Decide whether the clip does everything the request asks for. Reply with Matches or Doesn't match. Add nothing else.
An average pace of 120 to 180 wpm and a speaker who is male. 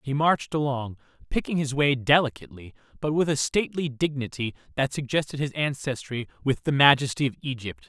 Matches